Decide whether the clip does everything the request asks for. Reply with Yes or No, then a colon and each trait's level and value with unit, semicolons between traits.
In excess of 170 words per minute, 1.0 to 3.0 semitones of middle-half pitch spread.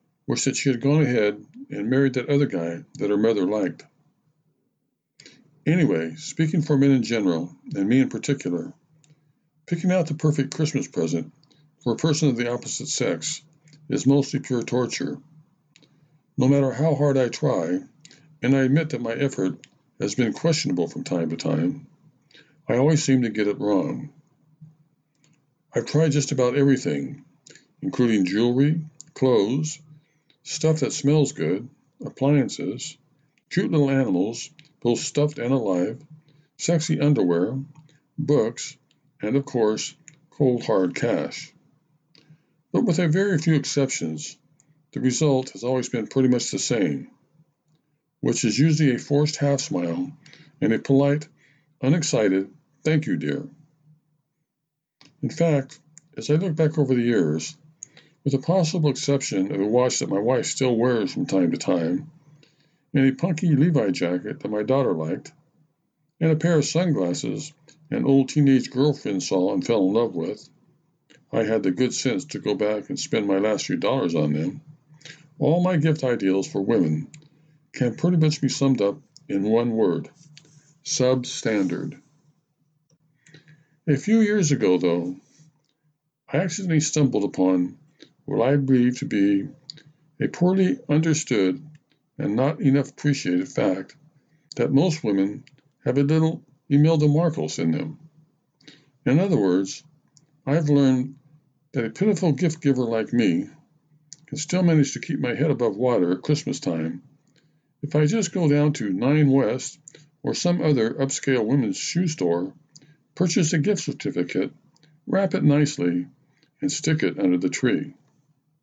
No: average, 145 wpm; narrow, 2.6 semitones